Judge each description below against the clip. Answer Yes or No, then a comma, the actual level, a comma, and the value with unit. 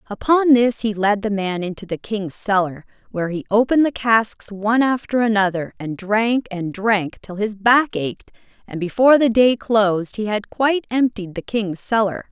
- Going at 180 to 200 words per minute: Yes, average, 185 wpm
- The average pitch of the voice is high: Yes, high, 215 Hz